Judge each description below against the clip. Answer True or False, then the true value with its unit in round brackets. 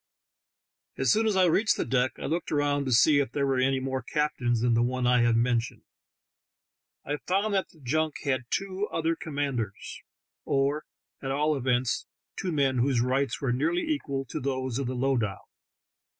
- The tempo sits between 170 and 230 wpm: True (180 wpm)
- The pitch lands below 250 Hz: True (135 Hz)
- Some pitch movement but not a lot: True (3.5 semitones)